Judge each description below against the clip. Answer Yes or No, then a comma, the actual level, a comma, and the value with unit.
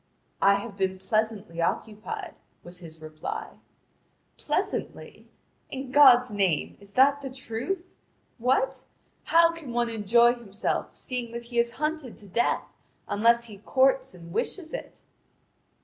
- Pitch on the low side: No, high, 235 Hz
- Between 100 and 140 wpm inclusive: Yes, slow, 135 wpm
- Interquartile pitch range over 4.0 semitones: Yes, average, 4.6 semitones